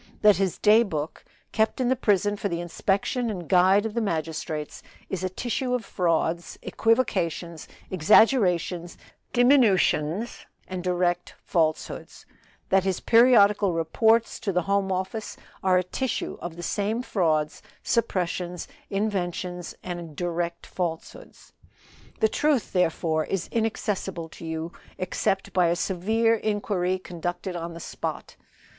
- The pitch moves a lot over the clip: No, average, 3.8 semitones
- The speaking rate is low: Yes, slow, 130 wpm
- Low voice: No, medium, 185 Hz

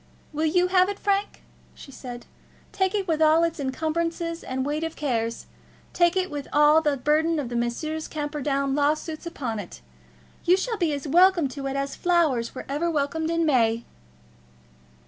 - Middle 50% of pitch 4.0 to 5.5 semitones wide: No, average, 3.4 semitones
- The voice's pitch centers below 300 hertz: No, very high, 310 Hz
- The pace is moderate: Yes, average, 170 wpm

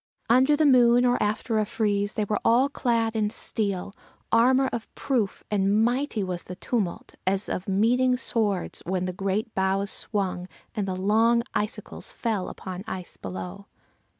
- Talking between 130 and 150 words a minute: No, average, 160 wpm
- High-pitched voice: Yes, high, 210 Hz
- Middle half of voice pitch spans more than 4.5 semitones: No, average, 3.7 semitones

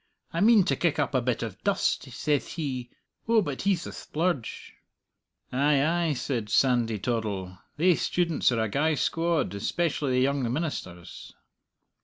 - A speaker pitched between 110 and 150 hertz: Yes, medium, 140 Hz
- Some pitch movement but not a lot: No, wide, 6.0 semitones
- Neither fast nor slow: Yes, average, 160 wpm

